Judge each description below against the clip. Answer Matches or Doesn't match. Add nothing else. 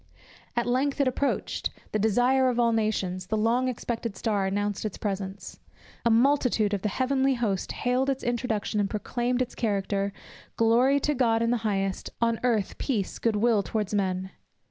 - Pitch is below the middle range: Doesn't match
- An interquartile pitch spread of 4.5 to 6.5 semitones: Doesn't match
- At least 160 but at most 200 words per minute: Matches